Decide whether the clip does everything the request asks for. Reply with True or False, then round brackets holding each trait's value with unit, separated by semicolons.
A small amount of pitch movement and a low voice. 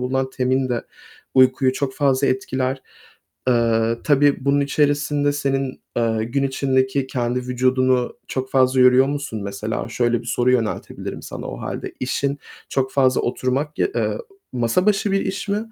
True (1.9 semitones; 130 Hz)